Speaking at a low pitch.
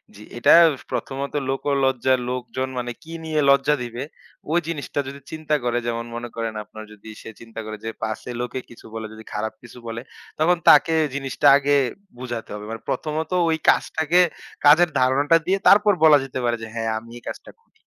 Yes: low, 130 Hz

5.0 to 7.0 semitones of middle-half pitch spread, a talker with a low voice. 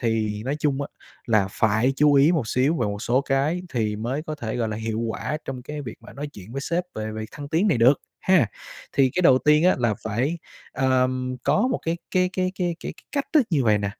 Yes: wide, 5.5 semitones; low, 130 Hz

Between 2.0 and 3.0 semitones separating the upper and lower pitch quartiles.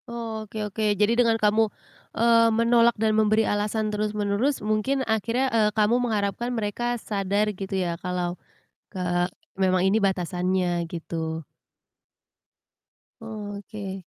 Yes: average, 2.7 semitones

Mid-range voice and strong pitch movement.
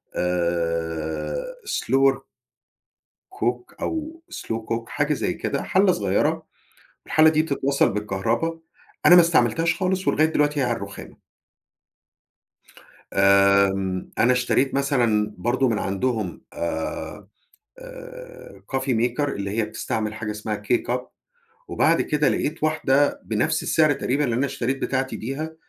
No: low, 125 Hz; wide, 6.3 semitones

